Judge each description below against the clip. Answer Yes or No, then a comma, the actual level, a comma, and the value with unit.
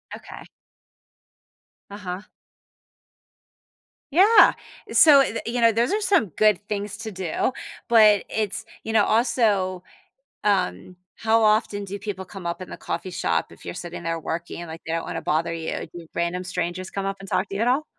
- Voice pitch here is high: Yes, high, 200 Hz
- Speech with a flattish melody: No, average, 3.7 semitones